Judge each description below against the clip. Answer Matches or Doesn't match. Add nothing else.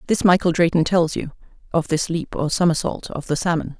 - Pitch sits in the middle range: Matches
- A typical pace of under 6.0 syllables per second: Matches